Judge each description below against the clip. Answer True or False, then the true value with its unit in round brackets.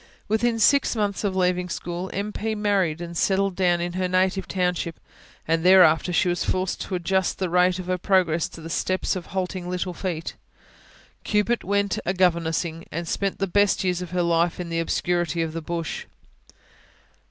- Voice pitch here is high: False (180 Hz)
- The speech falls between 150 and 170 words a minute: False (185 wpm)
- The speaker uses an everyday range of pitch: False (1.9 semitones)